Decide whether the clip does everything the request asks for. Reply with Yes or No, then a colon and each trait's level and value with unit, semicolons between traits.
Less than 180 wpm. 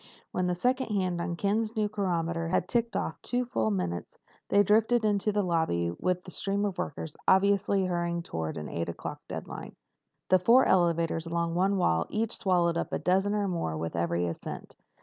No: average, 190 wpm